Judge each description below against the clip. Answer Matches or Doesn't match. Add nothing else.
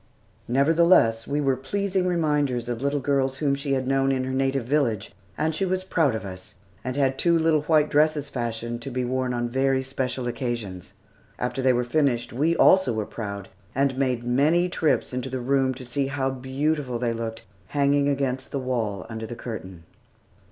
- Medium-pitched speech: Doesn't match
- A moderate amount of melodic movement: Matches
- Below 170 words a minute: Doesn't match